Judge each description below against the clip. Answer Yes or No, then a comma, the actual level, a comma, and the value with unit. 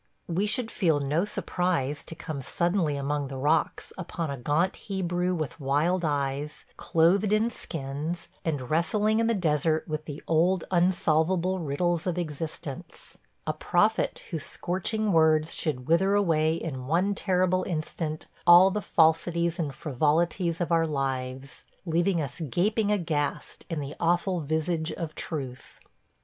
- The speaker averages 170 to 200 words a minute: No, average, 145 wpm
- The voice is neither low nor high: Yes, medium, 165 Hz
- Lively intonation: No, average, 3.3 semitones